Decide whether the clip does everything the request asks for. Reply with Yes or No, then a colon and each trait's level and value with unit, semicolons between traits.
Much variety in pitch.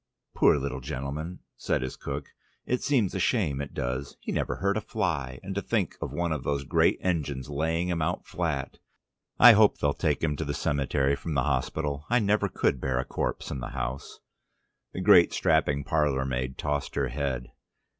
No: average, 4.4 semitones